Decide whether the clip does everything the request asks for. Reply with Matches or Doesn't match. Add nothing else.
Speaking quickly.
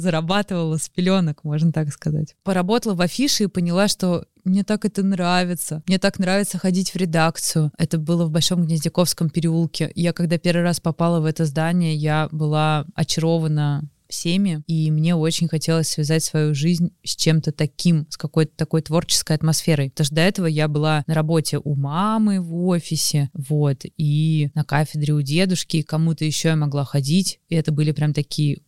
Matches